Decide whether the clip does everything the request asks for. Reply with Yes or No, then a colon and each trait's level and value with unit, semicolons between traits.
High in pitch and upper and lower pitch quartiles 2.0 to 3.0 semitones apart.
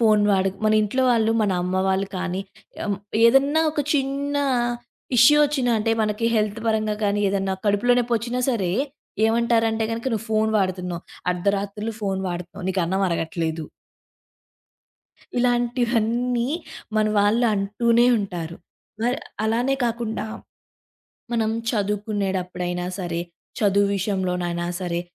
No: high, 210 Hz; average, 3.7 semitones